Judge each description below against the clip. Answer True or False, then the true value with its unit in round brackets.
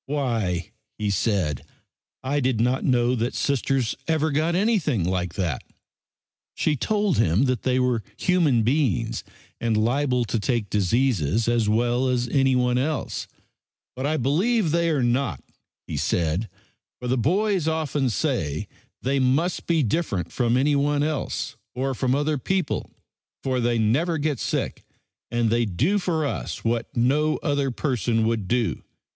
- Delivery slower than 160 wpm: True (150 wpm)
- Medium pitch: False (130 Hz)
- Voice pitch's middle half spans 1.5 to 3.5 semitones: False (4.4 semitones)